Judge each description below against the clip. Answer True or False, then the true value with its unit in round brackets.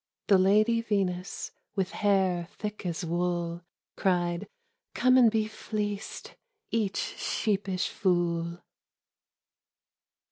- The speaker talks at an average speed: False (95 wpm)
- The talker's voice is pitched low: False (190 Hz)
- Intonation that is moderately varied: True (3.3 semitones)